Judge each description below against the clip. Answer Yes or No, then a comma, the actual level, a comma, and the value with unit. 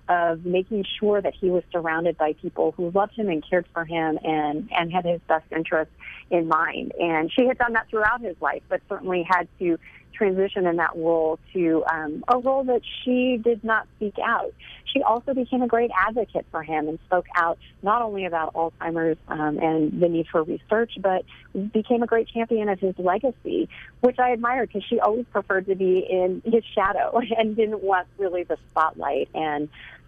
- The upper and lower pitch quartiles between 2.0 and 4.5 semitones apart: No, average, 5.2 semitones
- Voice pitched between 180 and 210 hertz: Yes, medium, 185 Hz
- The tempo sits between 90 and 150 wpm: No, average, 195 wpm